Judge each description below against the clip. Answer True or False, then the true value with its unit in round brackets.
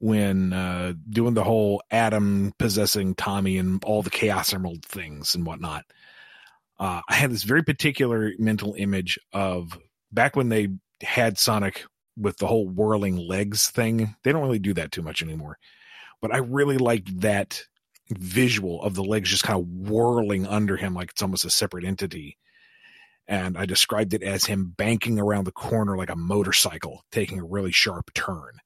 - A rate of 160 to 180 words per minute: True (175 wpm)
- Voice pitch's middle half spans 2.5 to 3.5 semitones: True (3.1 semitones)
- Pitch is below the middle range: True (100 Hz)